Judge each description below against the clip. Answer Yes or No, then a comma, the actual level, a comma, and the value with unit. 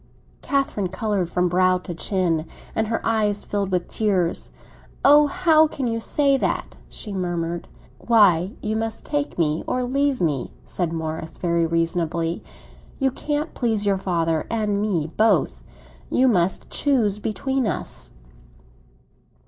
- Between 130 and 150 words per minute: Yes, average, 140 wpm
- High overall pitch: Yes, high, 200 Hz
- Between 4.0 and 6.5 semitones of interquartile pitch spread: Yes, wide, 5.6 semitones